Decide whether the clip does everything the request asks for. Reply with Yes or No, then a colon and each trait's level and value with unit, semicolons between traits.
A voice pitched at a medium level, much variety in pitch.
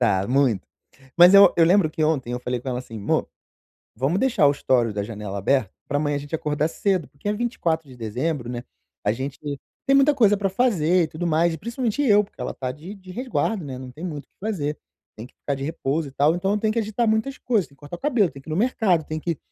Yes: medium, 160 Hz; wide, 7.0 semitones